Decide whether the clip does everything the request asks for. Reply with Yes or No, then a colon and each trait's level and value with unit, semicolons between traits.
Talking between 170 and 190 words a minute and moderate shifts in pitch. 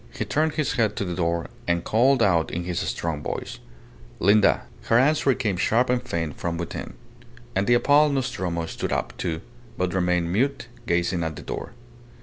No: average, 180 wpm; wide, 6.7 semitones